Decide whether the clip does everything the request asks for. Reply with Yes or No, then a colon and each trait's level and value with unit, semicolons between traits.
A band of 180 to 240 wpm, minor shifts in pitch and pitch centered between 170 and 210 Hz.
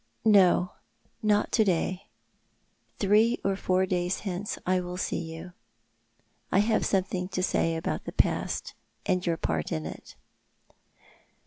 No: average, 140 wpm; narrow, 2.1 semitones; medium, 185 Hz